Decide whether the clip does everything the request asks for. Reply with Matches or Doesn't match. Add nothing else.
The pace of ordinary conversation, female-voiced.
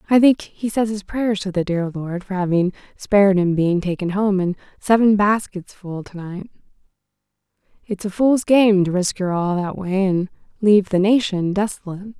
Matches